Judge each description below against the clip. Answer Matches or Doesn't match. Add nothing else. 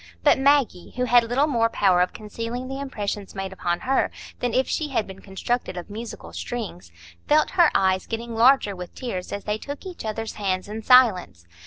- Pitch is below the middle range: Doesn't match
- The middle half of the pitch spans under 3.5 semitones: Doesn't match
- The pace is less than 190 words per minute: Doesn't match